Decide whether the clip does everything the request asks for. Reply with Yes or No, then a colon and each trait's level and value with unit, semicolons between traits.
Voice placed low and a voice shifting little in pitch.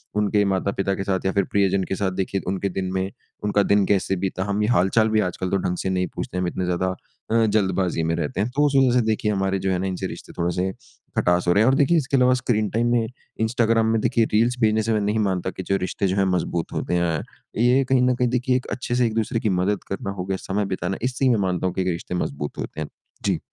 No: low, 100 Hz; average, 3.4 semitones